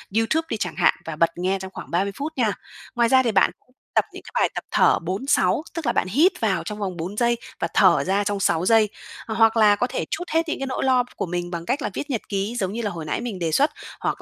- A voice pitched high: Yes, high, 215 Hz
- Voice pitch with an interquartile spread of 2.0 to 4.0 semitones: No, average, 5.0 semitones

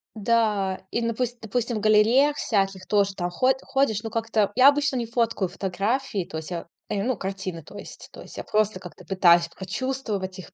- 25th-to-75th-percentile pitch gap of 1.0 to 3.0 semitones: No, average, 3.9 semitones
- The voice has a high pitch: Yes, high, 210 Hz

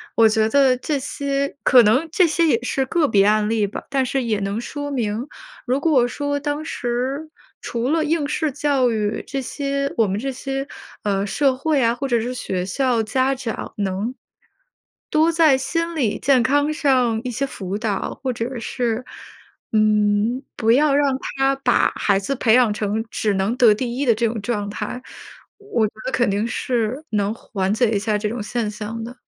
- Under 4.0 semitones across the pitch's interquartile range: No, average, 4.3 semitones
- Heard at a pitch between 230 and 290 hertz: Yes, high, 245 Hz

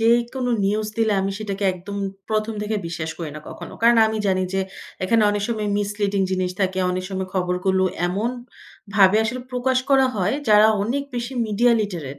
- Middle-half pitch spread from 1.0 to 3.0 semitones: No, average, 3.4 semitones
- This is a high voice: Yes, high, 205 Hz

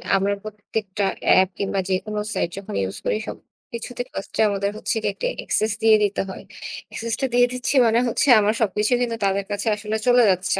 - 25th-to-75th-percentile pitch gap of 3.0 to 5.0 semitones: No, narrow, 2.5 semitones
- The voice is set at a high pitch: Yes, high, 210 Hz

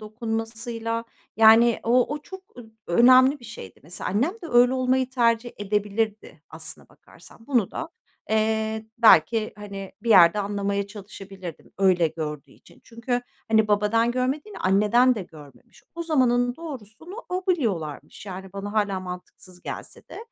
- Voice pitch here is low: No, high, 220 Hz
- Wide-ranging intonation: No, average, 3.7 semitones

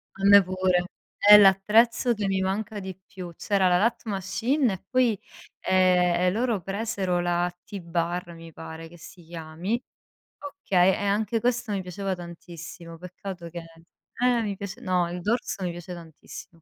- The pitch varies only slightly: No, average, 3.0 semitones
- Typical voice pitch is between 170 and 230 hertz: Yes, medium, 185 Hz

